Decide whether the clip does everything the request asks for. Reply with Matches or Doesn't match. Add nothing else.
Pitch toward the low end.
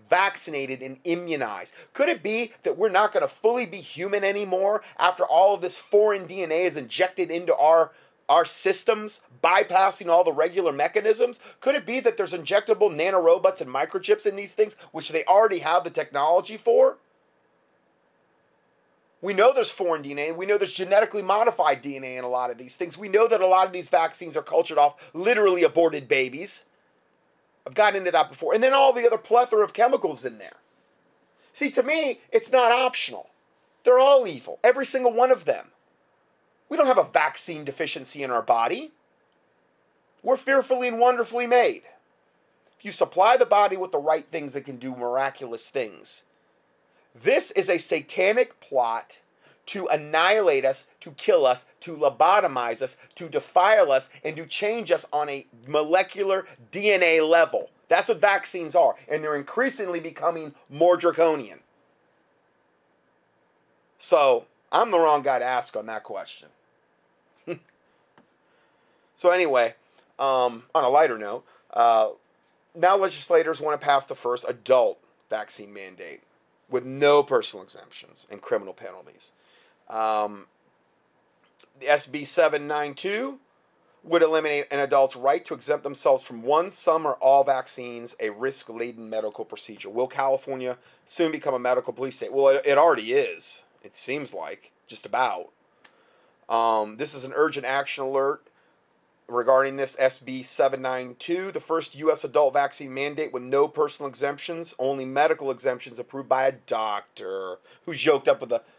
Doesn't match